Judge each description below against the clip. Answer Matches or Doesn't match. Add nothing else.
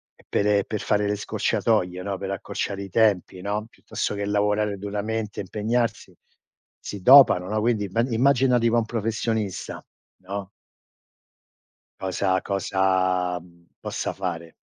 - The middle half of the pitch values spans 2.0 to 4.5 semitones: Matches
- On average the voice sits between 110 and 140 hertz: Doesn't match